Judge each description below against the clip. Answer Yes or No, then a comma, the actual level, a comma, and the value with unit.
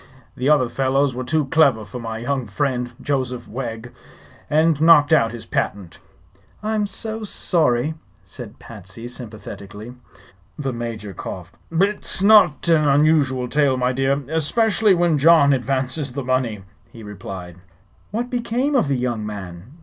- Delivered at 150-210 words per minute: No, average, 140 wpm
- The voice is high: No, low, 135 Hz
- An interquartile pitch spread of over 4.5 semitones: Yes, average, 5.3 semitones